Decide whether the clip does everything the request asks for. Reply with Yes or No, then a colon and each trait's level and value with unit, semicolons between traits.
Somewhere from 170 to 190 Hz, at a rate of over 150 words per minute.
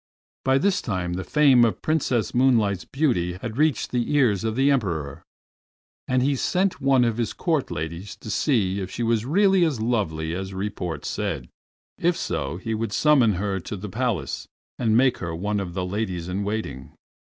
No: low, 110 Hz; average, 185 wpm